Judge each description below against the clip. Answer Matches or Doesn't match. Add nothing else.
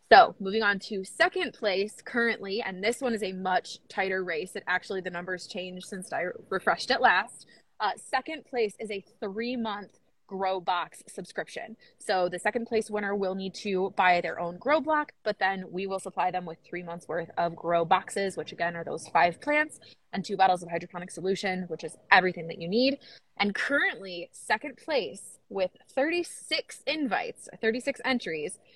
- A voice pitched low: Doesn't match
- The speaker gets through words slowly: Doesn't match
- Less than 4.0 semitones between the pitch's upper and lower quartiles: Doesn't match